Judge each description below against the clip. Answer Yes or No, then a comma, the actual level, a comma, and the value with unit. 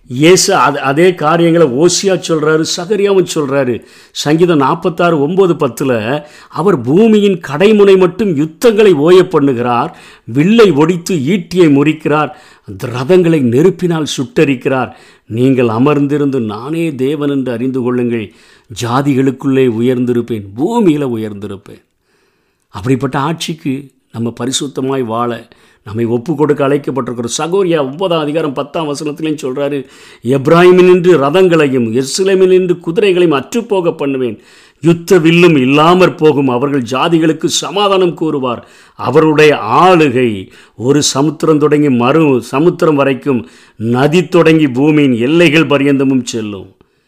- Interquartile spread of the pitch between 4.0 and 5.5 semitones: Yes, average, 4.7 semitones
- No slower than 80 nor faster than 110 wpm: Yes, average, 100 wpm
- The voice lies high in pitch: No, medium, 150 Hz